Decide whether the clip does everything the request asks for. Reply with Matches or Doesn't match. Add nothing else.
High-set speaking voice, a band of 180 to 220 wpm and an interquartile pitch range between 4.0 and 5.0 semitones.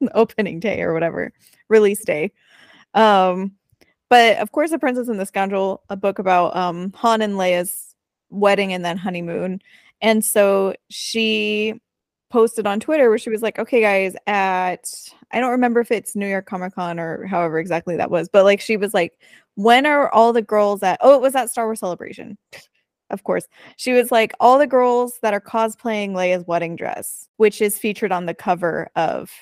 Doesn't match